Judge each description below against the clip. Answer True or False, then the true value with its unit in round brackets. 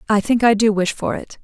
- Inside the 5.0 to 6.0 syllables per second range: True (5.6 syllables/s)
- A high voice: True (215 Hz)